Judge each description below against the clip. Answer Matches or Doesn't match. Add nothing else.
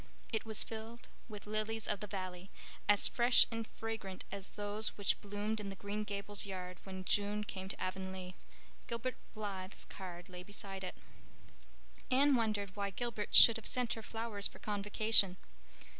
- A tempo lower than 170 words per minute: Matches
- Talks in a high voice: Matches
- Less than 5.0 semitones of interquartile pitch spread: Matches